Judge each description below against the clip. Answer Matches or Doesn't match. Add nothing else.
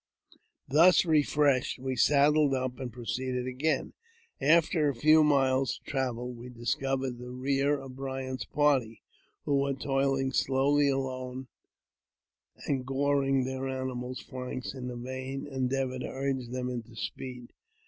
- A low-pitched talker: Matches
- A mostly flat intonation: Matches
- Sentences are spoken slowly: Matches